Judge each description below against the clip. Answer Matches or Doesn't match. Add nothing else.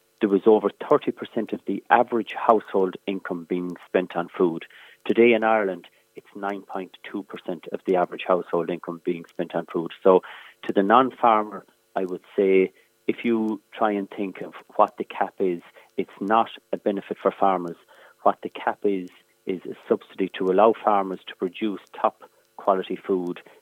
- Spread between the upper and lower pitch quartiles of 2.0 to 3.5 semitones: Matches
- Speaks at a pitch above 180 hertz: Doesn't match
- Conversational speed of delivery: Matches